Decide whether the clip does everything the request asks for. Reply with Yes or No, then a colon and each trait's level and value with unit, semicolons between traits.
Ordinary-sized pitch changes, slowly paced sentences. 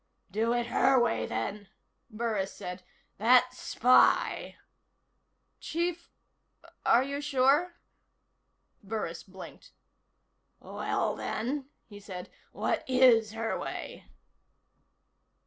Yes: average, 3.9 semitones; slow, 95 wpm